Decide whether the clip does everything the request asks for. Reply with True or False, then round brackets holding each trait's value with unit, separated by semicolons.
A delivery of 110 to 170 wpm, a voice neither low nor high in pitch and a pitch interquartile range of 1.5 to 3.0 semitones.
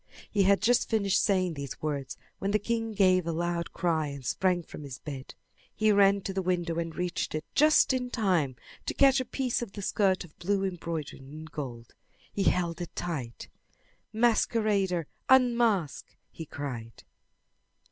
False (165 wpm; 180 Hz; 5.0 semitones)